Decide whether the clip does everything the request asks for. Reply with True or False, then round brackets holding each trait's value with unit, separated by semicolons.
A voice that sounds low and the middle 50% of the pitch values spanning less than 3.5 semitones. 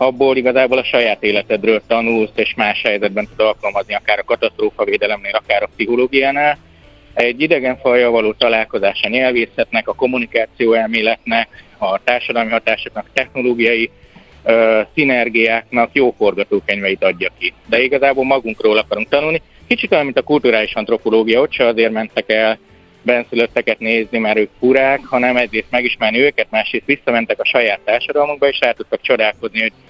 True (115 Hz; 2.9 semitones)